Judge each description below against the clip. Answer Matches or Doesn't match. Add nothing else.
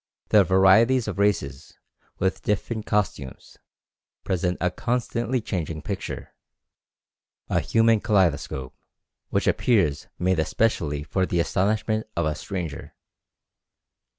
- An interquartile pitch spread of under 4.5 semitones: Doesn't match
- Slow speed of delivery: Matches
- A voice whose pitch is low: Matches